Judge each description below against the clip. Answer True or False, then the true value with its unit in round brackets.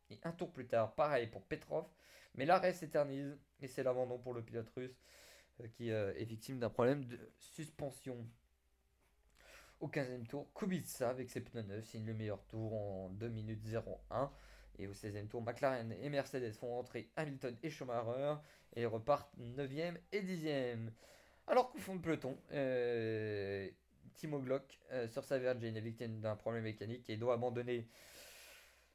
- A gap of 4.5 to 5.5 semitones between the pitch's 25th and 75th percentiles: False (3.8 semitones)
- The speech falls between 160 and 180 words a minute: True (170 wpm)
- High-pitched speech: False (120 Hz)